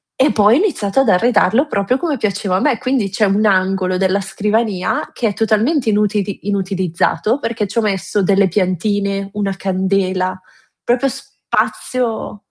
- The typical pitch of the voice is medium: No, high, 205 Hz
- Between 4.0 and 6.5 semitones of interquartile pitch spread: No, average, 3.1 semitones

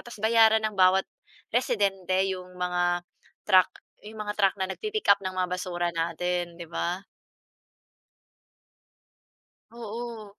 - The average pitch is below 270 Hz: Yes, high, 190 Hz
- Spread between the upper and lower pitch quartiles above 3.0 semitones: Yes, average, 3.4 semitones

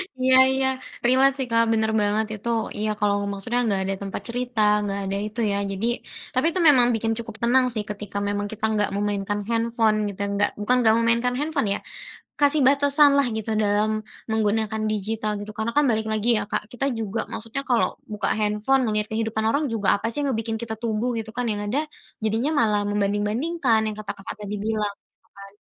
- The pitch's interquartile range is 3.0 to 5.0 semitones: No, narrow, 2.6 semitones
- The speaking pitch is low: No, high, 220 Hz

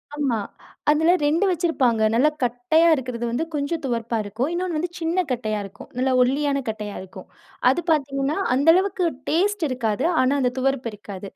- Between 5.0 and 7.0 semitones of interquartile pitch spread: Yes, wide, 5.5 semitones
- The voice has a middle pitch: No, very high, 270 Hz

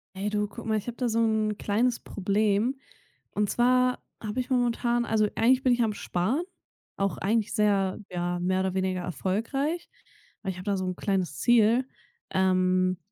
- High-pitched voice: Yes, high, 210 Hz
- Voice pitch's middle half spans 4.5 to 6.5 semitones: No, average, 4.1 semitones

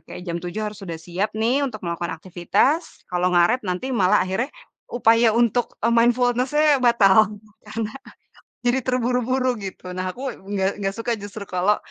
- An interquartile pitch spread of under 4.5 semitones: No, average, 4.8 semitones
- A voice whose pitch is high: Yes, high, 215 Hz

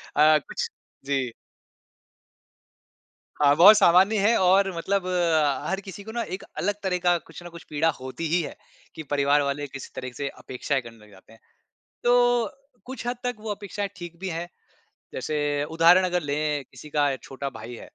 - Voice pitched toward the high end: No, medium, 165 Hz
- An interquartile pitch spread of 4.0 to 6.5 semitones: Yes, average, 5.1 semitones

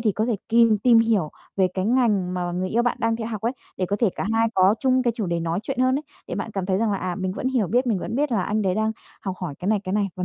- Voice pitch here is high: Yes, high, 210 Hz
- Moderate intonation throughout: Yes, average, 3.8 semitones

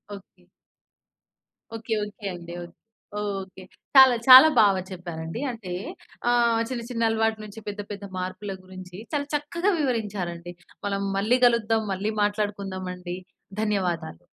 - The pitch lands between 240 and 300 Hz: No, high, 205 Hz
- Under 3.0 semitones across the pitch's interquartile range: No, average, 3.7 semitones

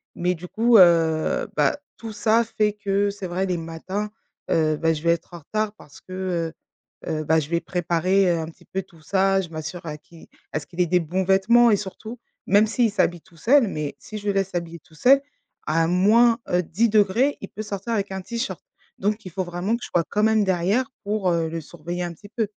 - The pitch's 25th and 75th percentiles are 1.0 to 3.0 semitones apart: No, average, 4.0 semitones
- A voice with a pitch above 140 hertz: Yes, high, 190 Hz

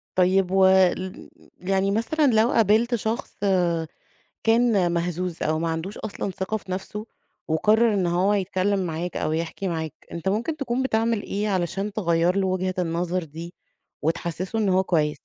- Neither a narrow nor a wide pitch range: Yes, average, 3.6 semitones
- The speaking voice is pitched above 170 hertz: Yes, high, 190 Hz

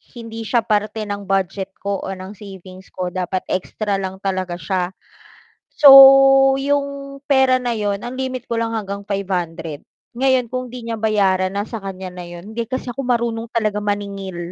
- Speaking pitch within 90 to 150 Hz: No, high, 205 Hz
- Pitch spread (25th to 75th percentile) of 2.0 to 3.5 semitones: No, average, 4.3 semitones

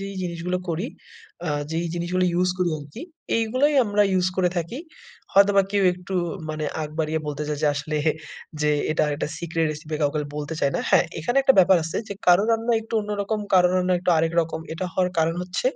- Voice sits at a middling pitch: Yes, medium, 180 Hz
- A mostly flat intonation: No, average, 3.7 semitones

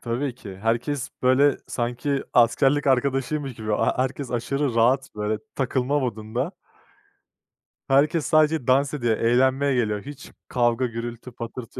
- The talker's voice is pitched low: Yes, low, 130 Hz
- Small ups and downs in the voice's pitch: No, average, 3.0 semitones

